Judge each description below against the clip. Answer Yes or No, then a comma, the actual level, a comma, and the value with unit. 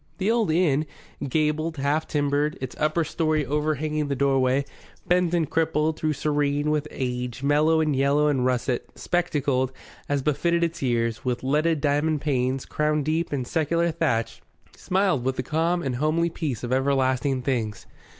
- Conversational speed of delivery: Yes, average, 160 wpm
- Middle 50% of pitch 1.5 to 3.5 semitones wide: Yes, average, 3.1 semitones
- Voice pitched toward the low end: No, medium, 150 Hz